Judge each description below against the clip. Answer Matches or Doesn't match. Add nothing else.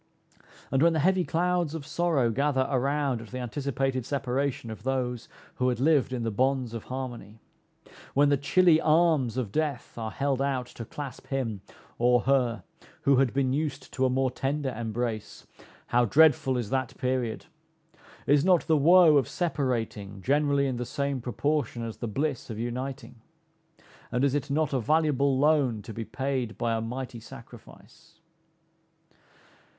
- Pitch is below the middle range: Matches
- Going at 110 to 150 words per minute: Doesn't match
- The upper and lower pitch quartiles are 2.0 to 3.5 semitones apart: Matches